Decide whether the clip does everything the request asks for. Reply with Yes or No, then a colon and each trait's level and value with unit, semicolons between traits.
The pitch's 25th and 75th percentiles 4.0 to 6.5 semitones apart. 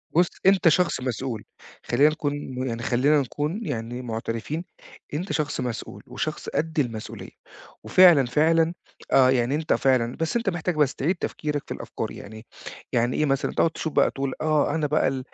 Yes: average, 4.3 semitones